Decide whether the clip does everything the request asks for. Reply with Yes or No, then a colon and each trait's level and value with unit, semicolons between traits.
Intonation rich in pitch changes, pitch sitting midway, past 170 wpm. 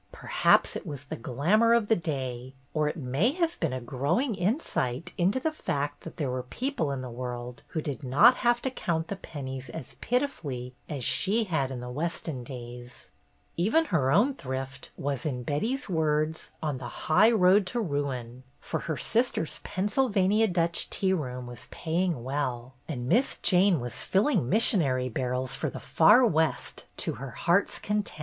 Yes: wide, 7.8 semitones; medium, 155 Hz; average, 180 wpm